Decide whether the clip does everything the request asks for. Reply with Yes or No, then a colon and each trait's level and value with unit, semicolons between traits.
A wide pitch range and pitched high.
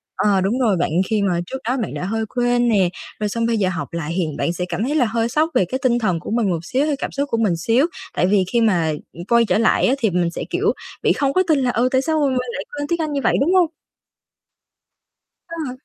Yes: wide, 6.4 semitones; high, 230 Hz